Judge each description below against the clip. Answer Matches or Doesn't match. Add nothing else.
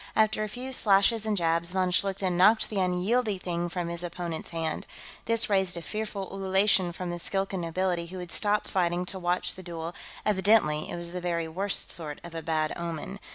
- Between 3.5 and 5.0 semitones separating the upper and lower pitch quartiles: Doesn't match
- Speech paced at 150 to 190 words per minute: Doesn't match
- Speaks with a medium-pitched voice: Matches